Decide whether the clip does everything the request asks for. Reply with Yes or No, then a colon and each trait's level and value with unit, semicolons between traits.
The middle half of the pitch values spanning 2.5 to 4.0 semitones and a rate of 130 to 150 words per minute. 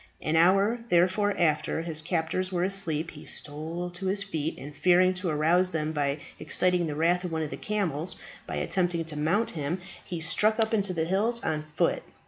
No: average, 3.1 semitones; average, 195 wpm